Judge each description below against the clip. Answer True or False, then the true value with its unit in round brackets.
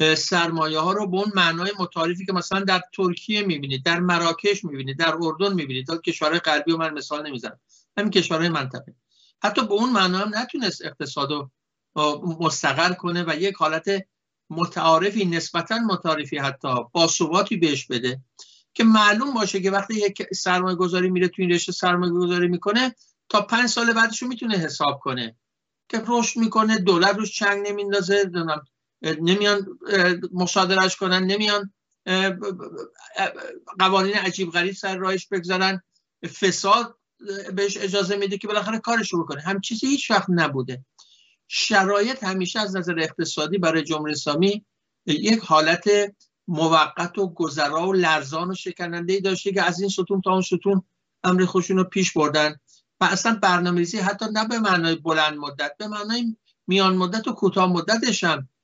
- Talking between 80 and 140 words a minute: False (150 wpm)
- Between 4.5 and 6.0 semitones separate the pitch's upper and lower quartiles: False (3.7 semitones)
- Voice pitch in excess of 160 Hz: True (185 Hz)